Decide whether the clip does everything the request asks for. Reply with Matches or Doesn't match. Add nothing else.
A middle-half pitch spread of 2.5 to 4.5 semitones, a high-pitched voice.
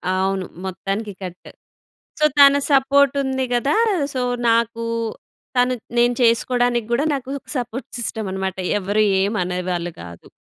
Doesn't match